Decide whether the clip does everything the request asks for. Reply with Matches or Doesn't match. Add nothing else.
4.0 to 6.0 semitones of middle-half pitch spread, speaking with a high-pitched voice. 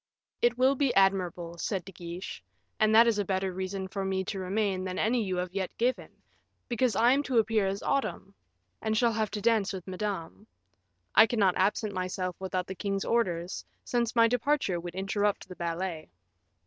Doesn't match